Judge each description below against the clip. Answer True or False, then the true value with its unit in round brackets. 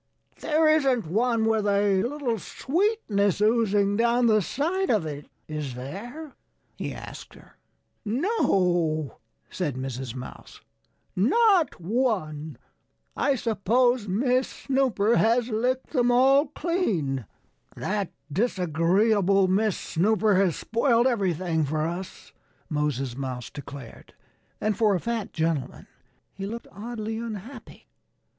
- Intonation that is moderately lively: False (6.4 semitones)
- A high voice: True (210 Hz)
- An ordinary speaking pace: False (115 wpm)